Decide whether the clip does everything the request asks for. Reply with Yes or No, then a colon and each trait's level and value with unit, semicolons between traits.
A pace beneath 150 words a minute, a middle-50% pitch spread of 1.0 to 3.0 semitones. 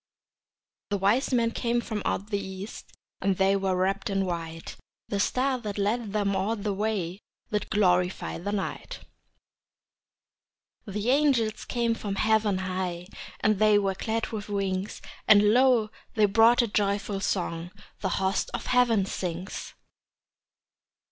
Yes: average, 140 wpm; narrow, 2.4 semitones